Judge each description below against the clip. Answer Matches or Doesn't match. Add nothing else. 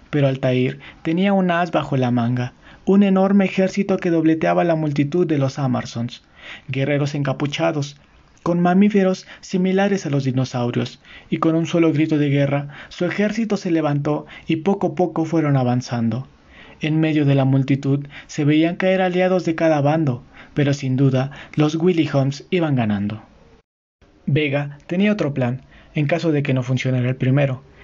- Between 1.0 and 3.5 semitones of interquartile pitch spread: Doesn't match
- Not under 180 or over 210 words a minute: Doesn't match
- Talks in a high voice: Doesn't match